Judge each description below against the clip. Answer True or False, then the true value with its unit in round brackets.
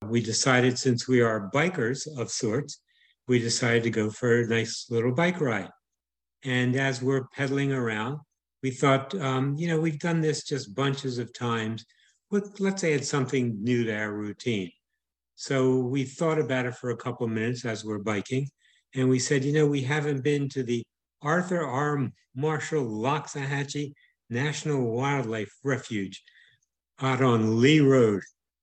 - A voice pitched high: False (130 Hz)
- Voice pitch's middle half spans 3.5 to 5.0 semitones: True (3.8 semitones)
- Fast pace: False (160 wpm)